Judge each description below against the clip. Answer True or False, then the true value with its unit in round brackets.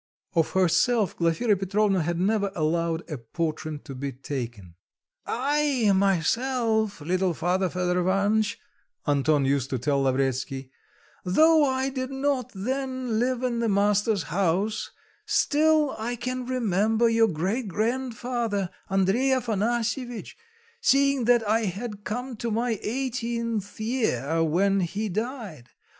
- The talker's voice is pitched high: True (210 Hz)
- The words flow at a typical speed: False (125 wpm)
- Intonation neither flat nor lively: False (5.9 semitones)